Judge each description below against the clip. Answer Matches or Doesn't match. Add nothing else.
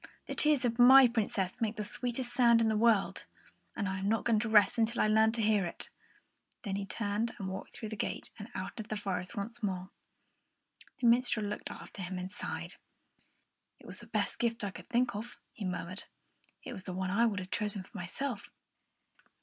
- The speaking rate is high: Matches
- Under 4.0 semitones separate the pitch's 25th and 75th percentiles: Matches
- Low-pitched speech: Doesn't match